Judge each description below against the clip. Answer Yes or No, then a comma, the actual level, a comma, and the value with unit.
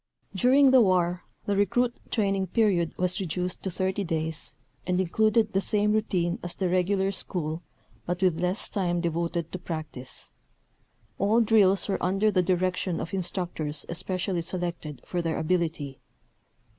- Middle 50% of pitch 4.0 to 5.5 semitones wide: No, narrow, 2.6 semitones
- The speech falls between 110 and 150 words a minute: Yes, average, 145 wpm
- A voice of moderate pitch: Yes, medium, 180 Hz